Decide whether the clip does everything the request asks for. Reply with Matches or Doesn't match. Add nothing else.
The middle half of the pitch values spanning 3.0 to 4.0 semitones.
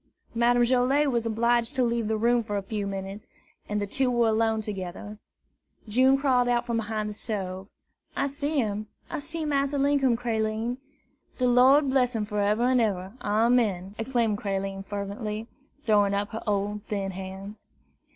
Matches